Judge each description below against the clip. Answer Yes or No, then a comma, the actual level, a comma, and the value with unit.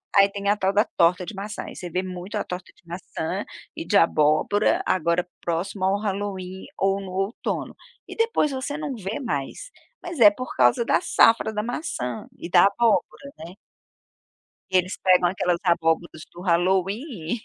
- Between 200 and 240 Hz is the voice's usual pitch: No, high, 190 Hz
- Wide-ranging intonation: No, average, 3.4 semitones